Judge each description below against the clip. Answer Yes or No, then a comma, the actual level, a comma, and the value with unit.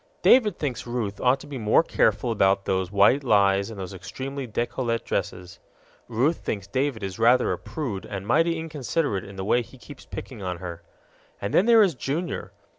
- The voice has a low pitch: Yes, low, 115 Hz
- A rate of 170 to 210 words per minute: Yes, average, 190 wpm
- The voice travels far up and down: Yes, wide, 6.0 semitones